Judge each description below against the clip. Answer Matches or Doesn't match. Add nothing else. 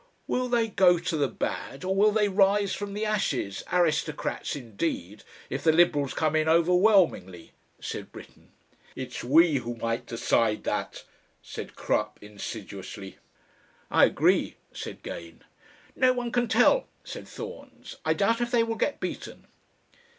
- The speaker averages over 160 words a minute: Doesn't match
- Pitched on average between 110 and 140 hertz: Doesn't match